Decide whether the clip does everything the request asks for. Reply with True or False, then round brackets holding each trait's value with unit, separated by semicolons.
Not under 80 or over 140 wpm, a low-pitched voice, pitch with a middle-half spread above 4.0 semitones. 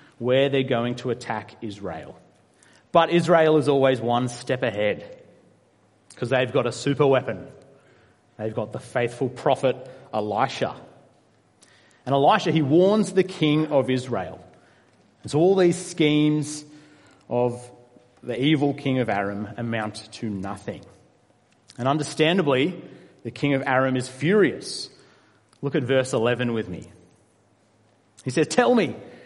True (135 wpm; 130 Hz; 4.6 semitones)